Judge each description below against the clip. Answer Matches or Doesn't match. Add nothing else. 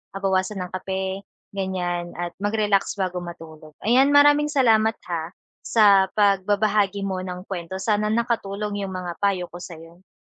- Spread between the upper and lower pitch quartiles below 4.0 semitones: Matches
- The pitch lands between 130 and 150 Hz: Doesn't match